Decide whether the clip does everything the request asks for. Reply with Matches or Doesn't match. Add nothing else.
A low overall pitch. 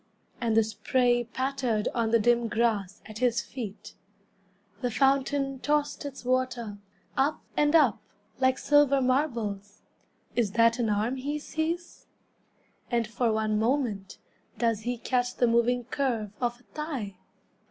Doesn't match